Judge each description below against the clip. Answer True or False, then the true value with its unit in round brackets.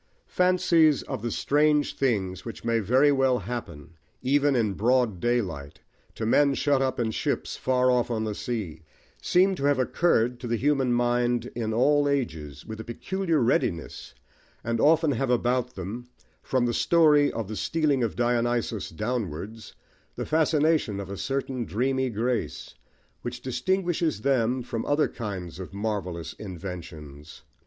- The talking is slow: False (155 wpm)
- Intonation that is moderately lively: True (4.5 semitones)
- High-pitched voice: False (120 Hz)